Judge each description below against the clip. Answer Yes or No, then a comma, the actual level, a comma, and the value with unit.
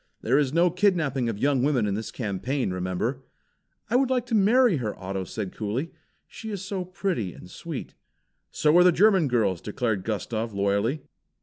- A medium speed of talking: Yes, average, 180 wpm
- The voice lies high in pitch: No, low, 135 Hz